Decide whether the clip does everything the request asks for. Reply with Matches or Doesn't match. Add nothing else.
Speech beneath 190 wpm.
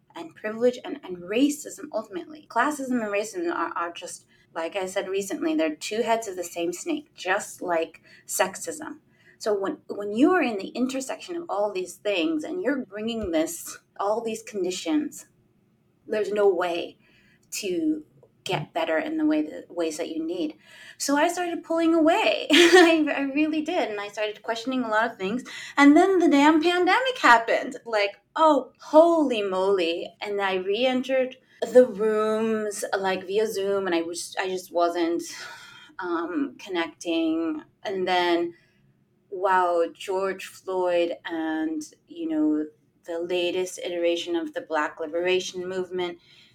Matches